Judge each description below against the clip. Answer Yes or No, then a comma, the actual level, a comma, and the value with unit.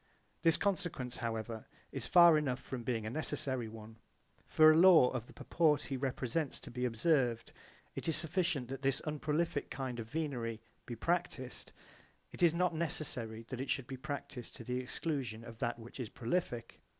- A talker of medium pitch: No, low, 130 Hz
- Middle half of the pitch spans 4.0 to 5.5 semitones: Yes, average, 4.9 semitones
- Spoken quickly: No, average, 175 wpm